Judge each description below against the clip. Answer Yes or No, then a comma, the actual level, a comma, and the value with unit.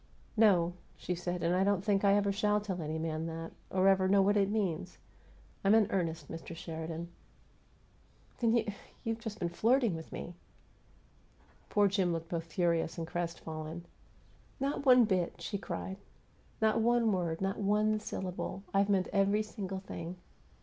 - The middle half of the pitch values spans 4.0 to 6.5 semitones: No, average, 3.6 semitones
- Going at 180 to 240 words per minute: No, average, 165 wpm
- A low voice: No, high, 190 Hz